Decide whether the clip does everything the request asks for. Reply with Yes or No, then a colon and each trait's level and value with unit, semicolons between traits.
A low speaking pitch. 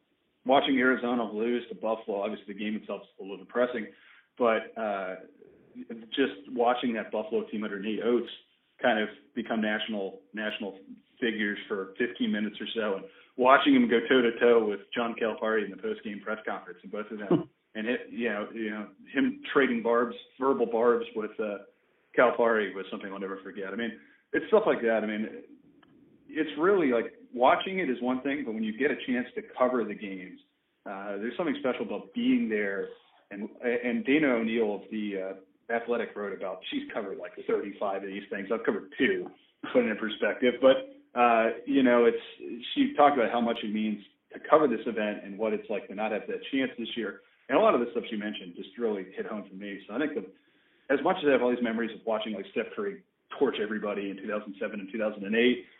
Yes: low, 115 Hz